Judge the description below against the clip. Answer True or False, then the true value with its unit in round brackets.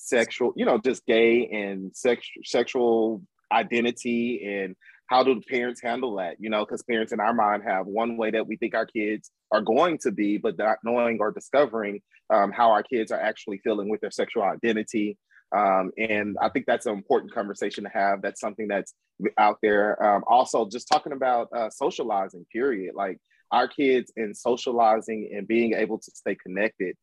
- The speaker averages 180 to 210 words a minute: True (190 wpm)